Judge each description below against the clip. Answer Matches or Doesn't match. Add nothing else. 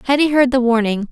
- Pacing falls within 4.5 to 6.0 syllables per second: Doesn't match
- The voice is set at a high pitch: Matches